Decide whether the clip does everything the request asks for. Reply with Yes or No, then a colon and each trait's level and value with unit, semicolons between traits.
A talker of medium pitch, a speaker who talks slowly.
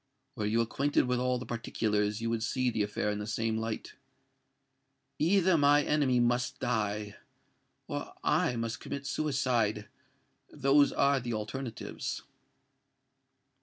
No: low, 120 Hz; slow, 130 wpm